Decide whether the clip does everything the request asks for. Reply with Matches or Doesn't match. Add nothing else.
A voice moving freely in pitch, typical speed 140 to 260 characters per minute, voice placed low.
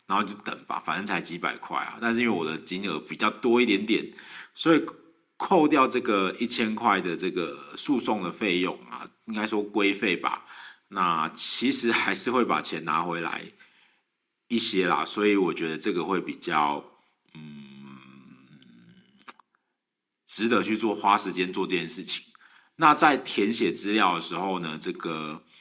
Matches